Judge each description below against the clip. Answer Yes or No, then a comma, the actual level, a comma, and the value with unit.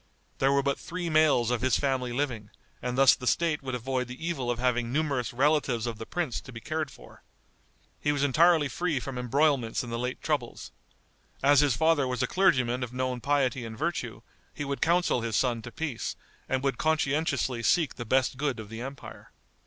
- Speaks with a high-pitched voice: No, low, 130 Hz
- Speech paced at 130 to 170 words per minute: No, average, 200 wpm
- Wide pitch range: No, average, 3.3 semitones